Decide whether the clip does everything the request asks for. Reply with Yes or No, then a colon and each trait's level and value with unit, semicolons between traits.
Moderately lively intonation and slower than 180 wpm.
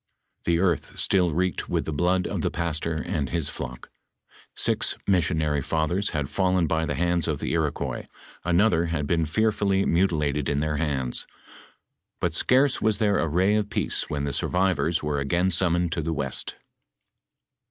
Yes: average, 3.4 semitones; average, 170 wpm